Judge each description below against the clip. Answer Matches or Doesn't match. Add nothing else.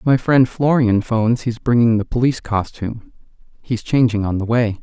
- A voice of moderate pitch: Doesn't match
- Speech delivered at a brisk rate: Doesn't match